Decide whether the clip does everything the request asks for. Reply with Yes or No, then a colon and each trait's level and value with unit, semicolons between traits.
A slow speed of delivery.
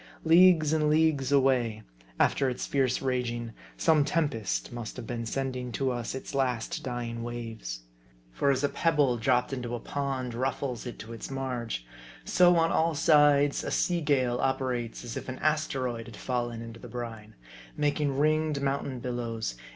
No: average, 165 wpm